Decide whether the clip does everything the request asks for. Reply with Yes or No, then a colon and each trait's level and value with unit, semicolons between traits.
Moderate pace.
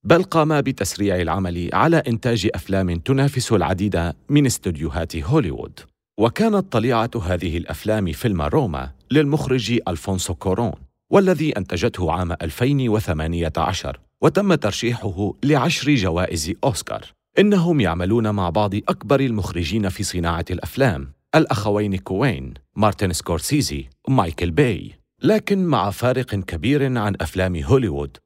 Yes: average, 110 wpm